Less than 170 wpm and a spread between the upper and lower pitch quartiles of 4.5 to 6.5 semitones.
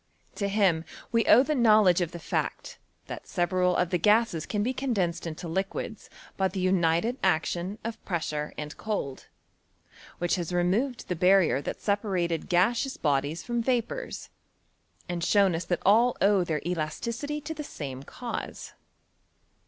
Yes: average, 150 wpm; average, 4.9 semitones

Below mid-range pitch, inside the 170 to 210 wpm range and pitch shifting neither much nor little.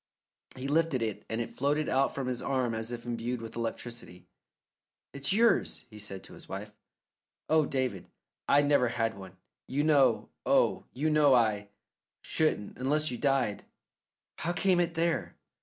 No: low, 130 Hz; average, 160 wpm; average, 4.7 semitones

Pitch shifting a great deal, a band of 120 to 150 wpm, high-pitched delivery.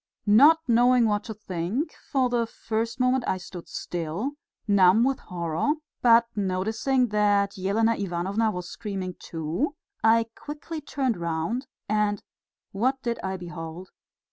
No: average, 4.8 semitones; slow, 135 wpm; high, 215 Hz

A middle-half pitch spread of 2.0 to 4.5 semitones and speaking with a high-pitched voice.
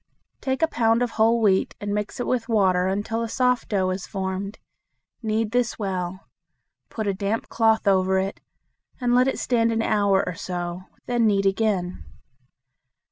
Yes: average, 3.2 semitones; high, 210 Hz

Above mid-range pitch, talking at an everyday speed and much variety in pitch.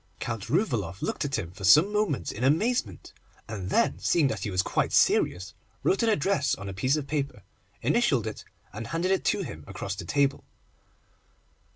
No: low, 135 Hz; average, 185 wpm; wide, 8.7 semitones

